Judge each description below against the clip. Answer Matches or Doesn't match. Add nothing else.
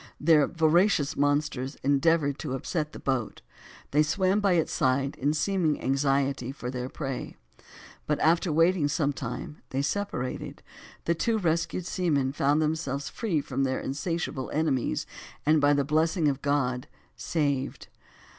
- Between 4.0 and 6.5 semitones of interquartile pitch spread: Doesn't match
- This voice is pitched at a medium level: Matches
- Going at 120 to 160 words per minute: Matches